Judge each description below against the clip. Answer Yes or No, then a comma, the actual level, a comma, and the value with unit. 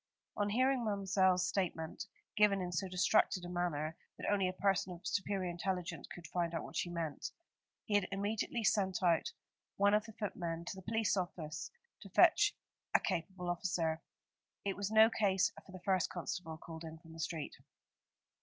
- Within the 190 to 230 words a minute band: No, average, 175 wpm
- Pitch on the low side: No, medium, 185 Hz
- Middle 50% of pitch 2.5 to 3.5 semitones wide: Yes, average, 3.0 semitones